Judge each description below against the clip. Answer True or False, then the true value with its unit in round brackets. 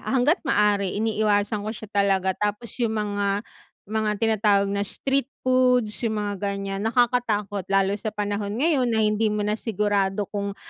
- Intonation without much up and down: True (1.7 semitones)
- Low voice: False (210 Hz)